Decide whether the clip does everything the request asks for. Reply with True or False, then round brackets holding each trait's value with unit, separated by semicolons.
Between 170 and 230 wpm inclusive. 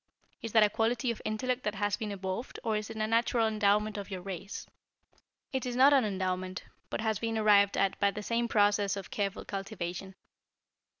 True (195 wpm)